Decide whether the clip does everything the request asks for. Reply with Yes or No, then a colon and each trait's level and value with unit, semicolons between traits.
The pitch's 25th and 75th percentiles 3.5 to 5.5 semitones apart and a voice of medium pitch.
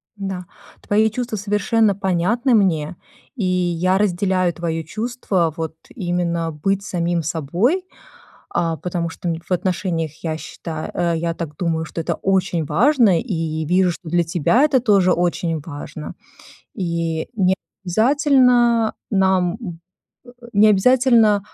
Yes: average, 4.0 semitones; medium, 180 Hz